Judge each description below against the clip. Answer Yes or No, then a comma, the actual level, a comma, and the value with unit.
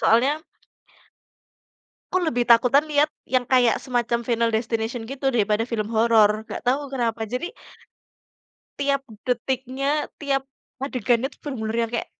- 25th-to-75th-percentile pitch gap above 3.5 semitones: No, average, 3.0 semitones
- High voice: Yes, high, 245 Hz